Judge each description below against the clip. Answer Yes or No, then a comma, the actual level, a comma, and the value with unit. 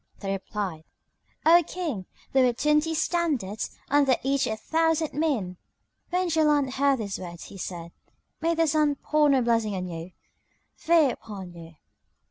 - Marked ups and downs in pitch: Yes, wide, 8.2 semitones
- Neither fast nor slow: Yes, average, 150 wpm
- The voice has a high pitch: Yes, very high, 270 Hz